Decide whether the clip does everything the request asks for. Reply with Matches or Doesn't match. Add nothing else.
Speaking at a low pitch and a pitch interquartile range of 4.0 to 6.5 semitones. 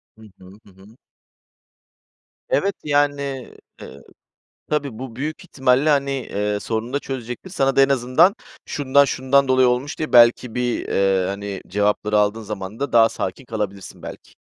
Matches